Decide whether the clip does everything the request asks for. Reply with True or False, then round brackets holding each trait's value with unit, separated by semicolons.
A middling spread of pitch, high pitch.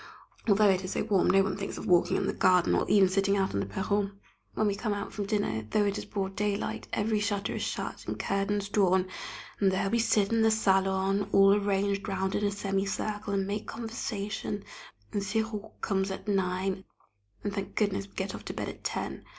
False (1.2 semitones; 200 Hz)